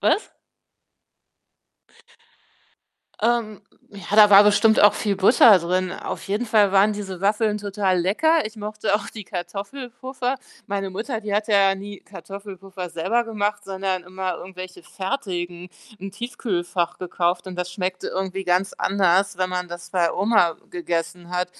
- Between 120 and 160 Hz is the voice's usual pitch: No, high, 195 Hz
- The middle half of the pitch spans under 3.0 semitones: Yes, narrow, 2.6 semitones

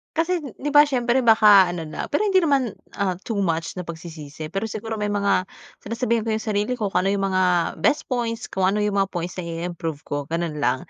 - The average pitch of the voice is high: Yes, high, 200 Hz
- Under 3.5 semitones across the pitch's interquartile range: No, average, 5.0 semitones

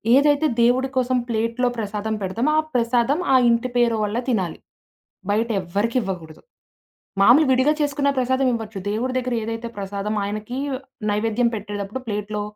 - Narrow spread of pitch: No, average, 3.4 semitones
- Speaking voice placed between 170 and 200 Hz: No, high, 230 Hz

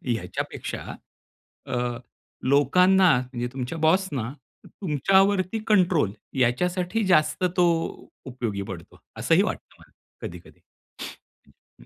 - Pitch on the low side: No, medium, 155 Hz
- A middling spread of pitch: No, wide, 7.0 semitones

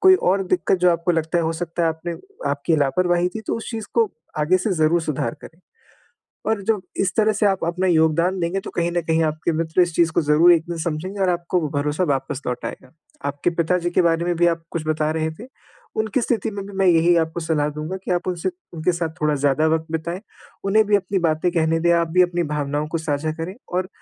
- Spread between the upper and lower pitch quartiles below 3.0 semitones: Yes, narrow, 2.5 semitones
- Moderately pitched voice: Yes, medium, 170 Hz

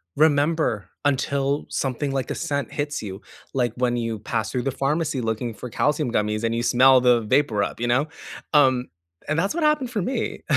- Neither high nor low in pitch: No, low, 130 Hz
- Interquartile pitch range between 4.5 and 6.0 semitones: No, average, 3.9 semitones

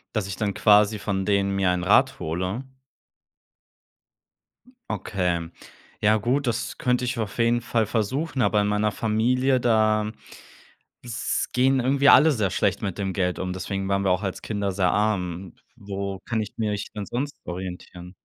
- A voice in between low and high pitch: No, low, 105 Hz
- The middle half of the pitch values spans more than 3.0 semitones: Yes, average, 3.5 semitones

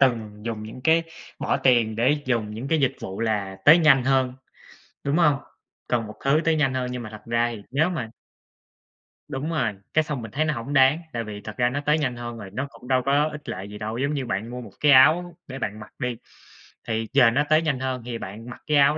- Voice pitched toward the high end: No, low, 130 Hz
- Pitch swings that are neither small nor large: Yes, average, 4.3 semitones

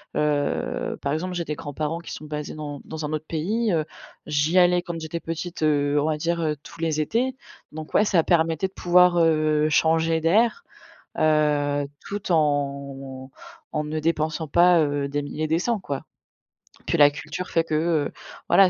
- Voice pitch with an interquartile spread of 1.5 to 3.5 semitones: Yes, narrow, 2.4 semitones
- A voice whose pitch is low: No, medium, 155 Hz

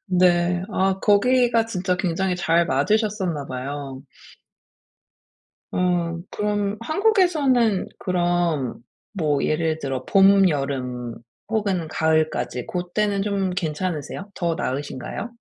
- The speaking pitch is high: No, medium, 180 Hz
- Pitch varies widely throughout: No, average, 4.6 semitones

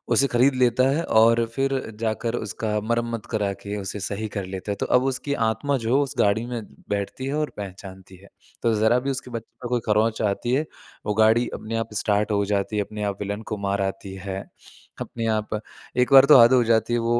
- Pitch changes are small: No, average, 3.1 semitones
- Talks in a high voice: No, low, 110 Hz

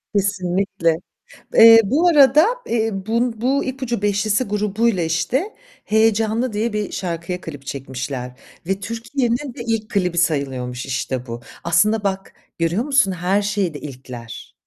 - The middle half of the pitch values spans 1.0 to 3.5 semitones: No, wide, 5.5 semitones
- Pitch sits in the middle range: No, high, 200 Hz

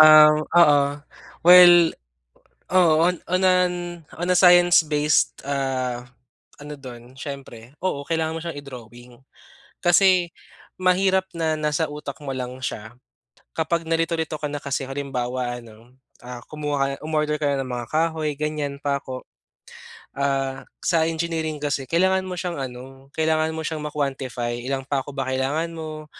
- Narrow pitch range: No, average, 3.4 semitones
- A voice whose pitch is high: No, medium, 150 Hz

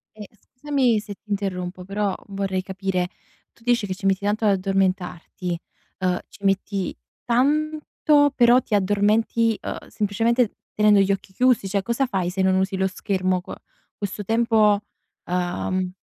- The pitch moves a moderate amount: Yes, average, 3.2 semitones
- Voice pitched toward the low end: No, high, 200 Hz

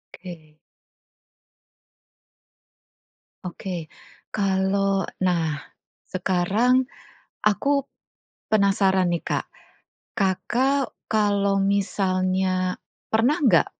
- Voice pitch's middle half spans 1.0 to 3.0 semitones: Yes, narrow, 2.5 semitones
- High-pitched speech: Yes, high, 195 Hz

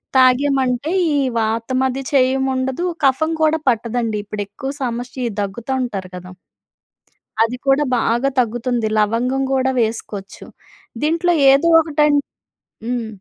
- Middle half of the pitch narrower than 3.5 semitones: Yes, average, 2.9 semitones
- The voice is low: No, very high, 250 Hz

